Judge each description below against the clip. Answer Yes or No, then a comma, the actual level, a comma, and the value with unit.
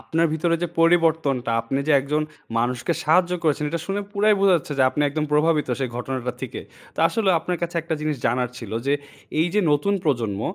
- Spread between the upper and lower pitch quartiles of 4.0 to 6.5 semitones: Yes, average, 4.5 semitones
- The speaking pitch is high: No, medium, 155 Hz